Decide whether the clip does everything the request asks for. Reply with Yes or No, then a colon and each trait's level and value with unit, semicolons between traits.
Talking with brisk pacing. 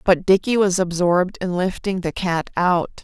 No: average, 180 wpm